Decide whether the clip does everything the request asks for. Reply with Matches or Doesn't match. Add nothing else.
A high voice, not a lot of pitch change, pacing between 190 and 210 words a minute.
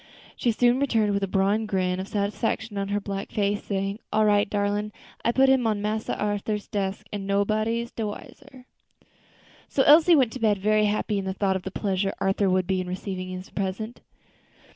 Matches